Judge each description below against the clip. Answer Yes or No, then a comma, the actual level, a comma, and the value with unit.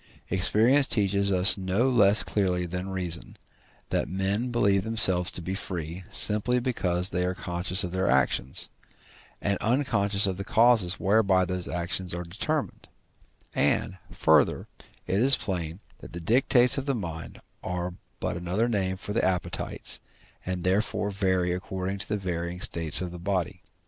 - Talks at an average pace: Yes, average, 155 wpm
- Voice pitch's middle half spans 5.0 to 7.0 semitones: No, average, 2.8 semitones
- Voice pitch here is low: Yes, very low, 95 Hz